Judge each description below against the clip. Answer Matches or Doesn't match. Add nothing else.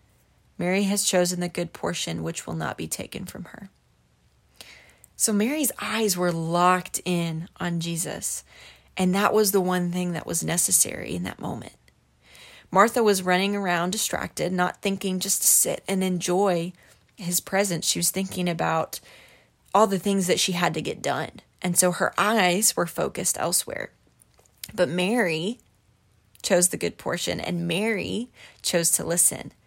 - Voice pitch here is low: Doesn't match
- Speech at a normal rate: Matches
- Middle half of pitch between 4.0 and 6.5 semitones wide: Doesn't match